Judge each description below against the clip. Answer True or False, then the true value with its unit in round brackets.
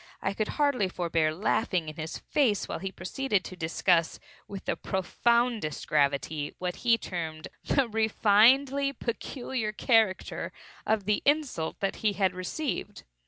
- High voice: True (205 Hz)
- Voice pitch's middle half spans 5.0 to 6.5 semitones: True (5.4 semitones)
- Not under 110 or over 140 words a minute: True (135 wpm)